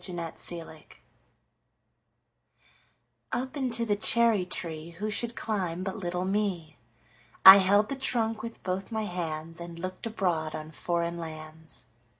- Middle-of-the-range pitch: Yes, medium, 180 Hz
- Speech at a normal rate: No, slow, 120 wpm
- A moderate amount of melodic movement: Yes, average, 4.5 semitones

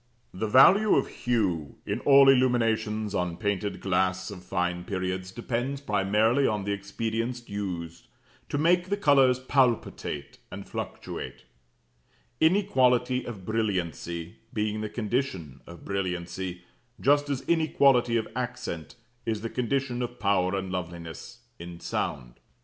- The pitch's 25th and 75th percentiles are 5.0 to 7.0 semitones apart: Yes, wide, 5.6 semitones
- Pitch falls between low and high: No, low, 110 Hz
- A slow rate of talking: Yes, slow, 125 wpm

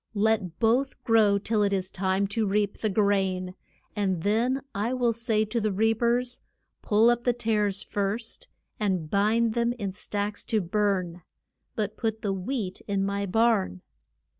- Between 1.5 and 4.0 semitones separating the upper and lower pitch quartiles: Yes, narrow, 2.5 semitones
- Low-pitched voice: No, high, 210 Hz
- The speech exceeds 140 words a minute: Yes, average, 165 wpm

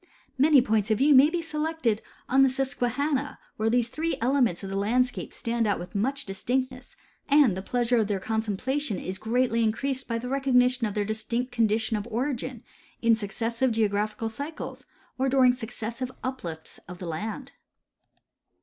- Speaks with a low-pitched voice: No, high, 240 Hz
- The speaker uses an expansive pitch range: No, average, 3.5 semitones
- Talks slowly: No, average, 165 wpm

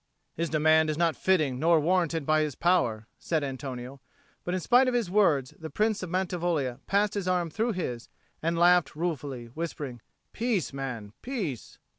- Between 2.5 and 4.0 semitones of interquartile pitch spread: No, average, 4.9 semitones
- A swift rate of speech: No, average, 170 wpm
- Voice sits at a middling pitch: Yes, medium, 165 Hz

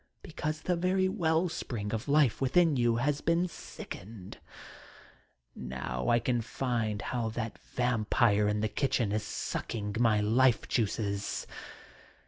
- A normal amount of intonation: No, wide, 5.8 semitones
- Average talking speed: No, slow, 130 wpm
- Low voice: Yes, low, 120 Hz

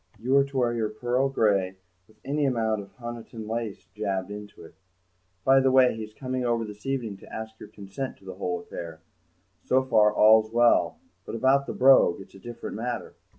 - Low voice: Yes, low, 115 Hz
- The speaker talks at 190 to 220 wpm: Yes, average, 195 wpm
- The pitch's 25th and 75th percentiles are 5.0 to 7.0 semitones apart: No, average, 3.6 semitones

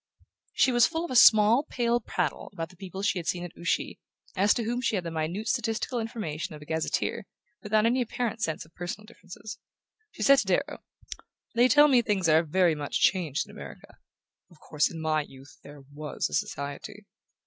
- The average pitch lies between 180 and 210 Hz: Yes, high, 190 Hz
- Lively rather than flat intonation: Yes, wide, 6.5 semitones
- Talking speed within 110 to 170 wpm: No, average, 195 wpm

